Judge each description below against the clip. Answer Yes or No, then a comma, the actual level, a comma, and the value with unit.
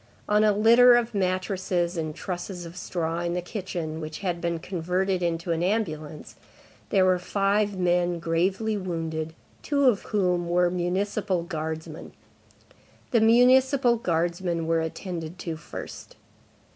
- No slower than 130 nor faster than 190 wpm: Yes, slow, 135 wpm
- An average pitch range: Yes, average, 3.3 semitones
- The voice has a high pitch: No, medium, 180 Hz